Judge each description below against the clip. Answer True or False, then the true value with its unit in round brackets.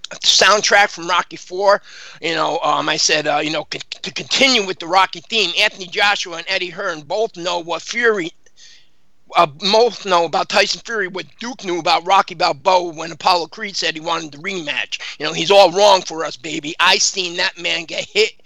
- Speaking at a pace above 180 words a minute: True (200 wpm)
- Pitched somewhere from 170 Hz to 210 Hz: True (190 Hz)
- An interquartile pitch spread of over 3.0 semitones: True (3.4 semitones)